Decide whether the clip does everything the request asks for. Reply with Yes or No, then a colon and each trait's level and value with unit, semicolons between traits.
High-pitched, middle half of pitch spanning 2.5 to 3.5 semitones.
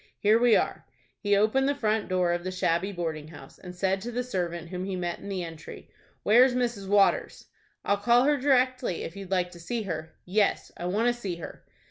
No: high, 195 Hz; average, 5.1 semitones